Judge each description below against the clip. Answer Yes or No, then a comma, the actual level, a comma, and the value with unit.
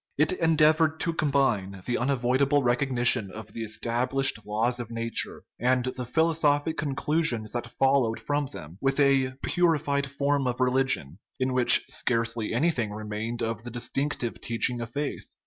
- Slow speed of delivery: No, average, 145 wpm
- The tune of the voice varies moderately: Yes, average, 3.5 semitones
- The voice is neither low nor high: No, low, 130 Hz